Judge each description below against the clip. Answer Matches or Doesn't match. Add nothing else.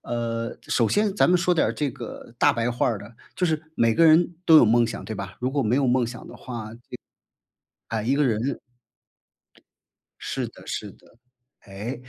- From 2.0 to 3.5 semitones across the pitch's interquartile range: Doesn't match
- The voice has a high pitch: Doesn't match